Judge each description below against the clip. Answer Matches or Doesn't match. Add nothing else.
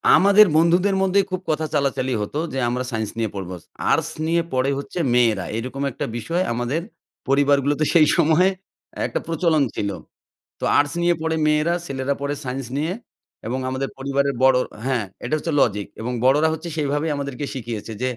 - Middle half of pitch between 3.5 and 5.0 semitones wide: Matches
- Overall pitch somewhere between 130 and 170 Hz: Matches